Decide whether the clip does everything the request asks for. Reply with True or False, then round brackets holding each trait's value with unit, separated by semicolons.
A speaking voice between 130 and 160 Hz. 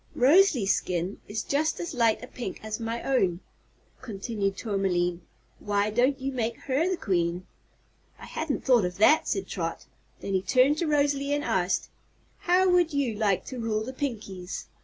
False (230 Hz)